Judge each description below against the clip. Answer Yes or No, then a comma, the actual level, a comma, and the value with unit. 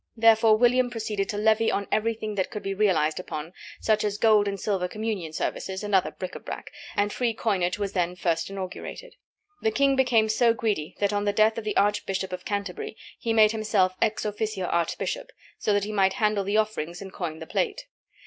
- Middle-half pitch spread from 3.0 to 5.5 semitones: No, narrow, 2.5 semitones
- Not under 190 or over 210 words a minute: Yes, fast, 205 wpm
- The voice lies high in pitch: Yes, high, 210 Hz